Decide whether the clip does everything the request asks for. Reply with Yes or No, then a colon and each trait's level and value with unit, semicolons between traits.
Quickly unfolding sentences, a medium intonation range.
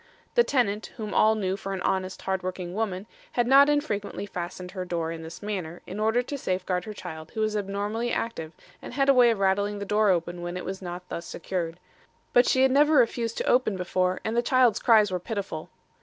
Yes: fast, 220 wpm; average, 4.1 semitones